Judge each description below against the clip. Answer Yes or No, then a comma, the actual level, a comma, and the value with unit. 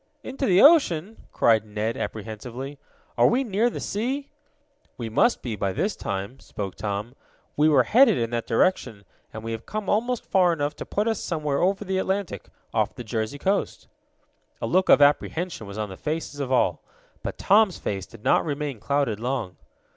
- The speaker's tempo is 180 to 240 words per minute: Yes, average, 185 wpm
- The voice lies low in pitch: No, medium, 145 Hz